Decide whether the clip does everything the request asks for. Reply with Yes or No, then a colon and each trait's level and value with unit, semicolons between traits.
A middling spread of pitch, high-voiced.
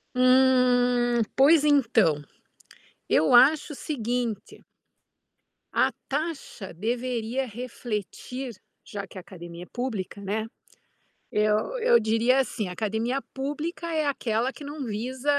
Yes: average, 3.9 semitones; high, 245 Hz